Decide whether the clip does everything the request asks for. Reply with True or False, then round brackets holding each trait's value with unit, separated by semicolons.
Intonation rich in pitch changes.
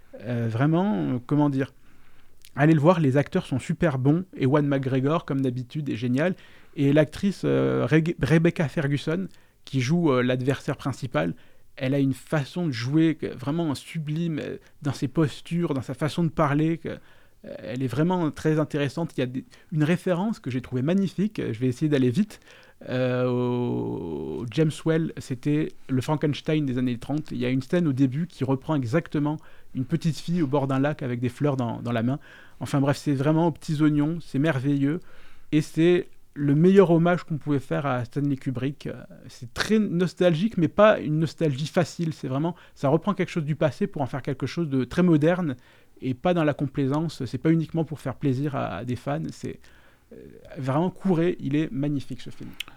False (3.6 semitones)